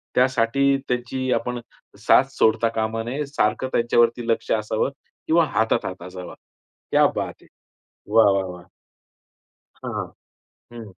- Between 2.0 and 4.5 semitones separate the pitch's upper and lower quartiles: Yes, average, 2.8 semitones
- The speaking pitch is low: Yes, low, 115 Hz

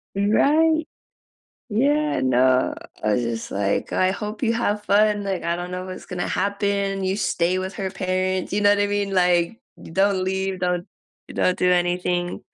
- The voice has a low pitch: No, high, 190 Hz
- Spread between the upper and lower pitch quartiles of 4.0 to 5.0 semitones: No, narrow, 2.4 semitones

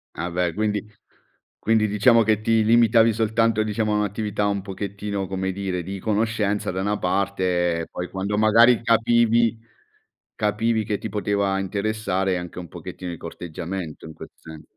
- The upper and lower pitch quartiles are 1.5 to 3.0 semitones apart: Yes, average, 2.7 semitones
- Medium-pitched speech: No, low, 100 Hz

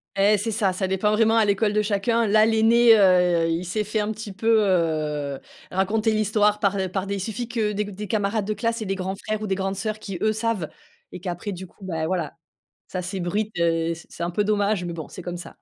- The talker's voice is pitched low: No, high, 200 Hz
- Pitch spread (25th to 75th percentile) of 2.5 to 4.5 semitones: Yes, average, 2.9 semitones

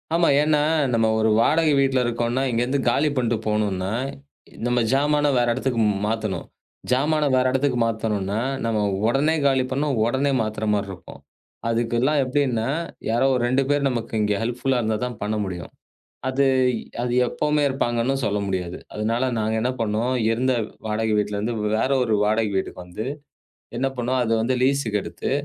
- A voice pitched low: Yes, low, 120 Hz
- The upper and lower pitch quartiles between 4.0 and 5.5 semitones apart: No, average, 3.6 semitones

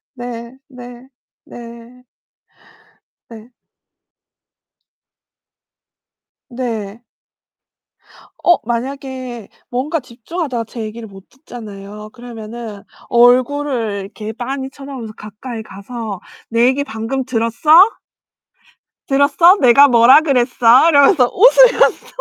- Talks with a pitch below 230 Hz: No, high, 245 Hz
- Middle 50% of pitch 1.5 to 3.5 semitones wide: Yes, average, 2.9 semitones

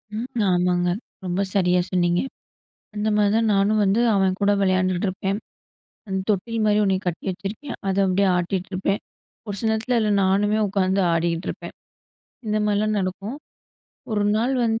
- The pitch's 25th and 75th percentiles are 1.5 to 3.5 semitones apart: Yes, narrow, 2.4 semitones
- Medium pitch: No, high, 195 Hz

